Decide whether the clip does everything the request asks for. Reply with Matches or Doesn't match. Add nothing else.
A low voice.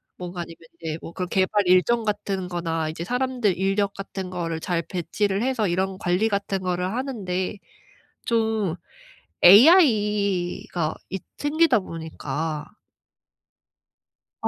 Doesn't match